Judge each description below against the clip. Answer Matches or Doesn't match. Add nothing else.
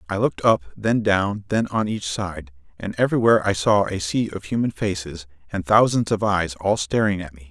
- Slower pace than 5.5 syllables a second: Matches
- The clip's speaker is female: Doesn't match